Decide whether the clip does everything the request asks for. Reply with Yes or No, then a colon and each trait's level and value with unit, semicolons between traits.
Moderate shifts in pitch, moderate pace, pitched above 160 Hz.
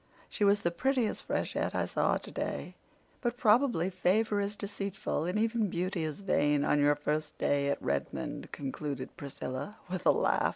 No: wide, 6.2 semitones; average, 165 wpm; medium, 185 Hz